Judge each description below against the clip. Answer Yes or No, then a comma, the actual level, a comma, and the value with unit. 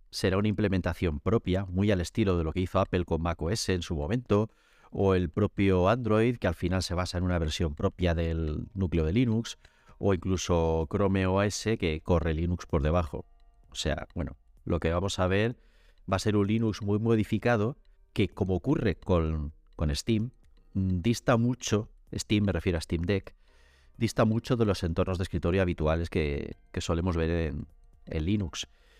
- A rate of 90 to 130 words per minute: No, average, 180 wpm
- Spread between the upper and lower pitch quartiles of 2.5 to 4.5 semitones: Yes, average, 3.7 semitones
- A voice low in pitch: Yes, very low, 95 Hz